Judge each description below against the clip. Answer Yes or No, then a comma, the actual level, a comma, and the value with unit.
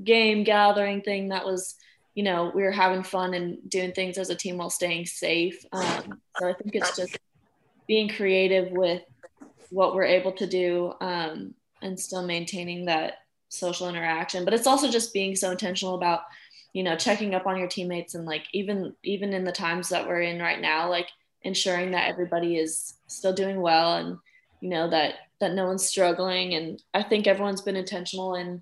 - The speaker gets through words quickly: No, average, 195 wpm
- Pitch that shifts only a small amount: Yes, narrow, 1.8 semitones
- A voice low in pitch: No, medium, 185 Hz